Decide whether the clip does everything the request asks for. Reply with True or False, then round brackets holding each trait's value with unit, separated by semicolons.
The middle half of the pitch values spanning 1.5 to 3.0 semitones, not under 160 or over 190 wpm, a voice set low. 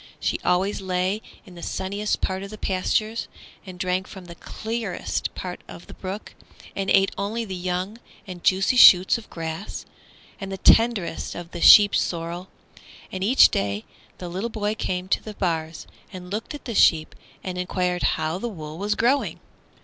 False (2.7 semitones; 175 wpm; 190 Hz)